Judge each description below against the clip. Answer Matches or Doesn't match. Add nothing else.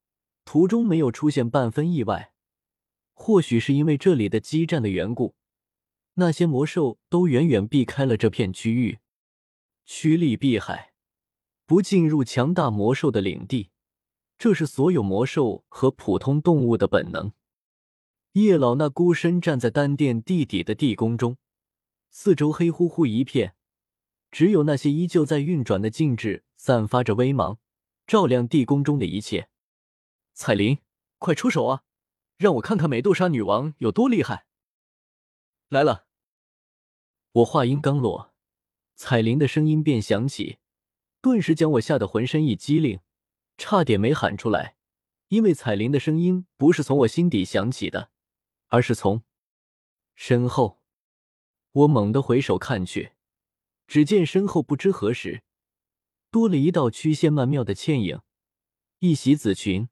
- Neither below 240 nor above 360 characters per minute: Doesn't match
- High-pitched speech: Doesn't match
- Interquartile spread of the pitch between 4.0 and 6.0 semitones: Doesn't match